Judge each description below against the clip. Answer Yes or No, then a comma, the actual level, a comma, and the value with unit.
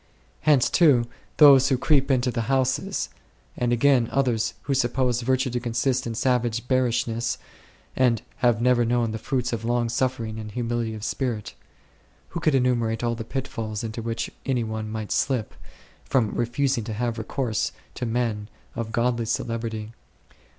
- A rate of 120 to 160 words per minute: No, average, 170 wpm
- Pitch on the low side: Yes, low, 120 Hz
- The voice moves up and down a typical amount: No, narrow, 2.2 semitones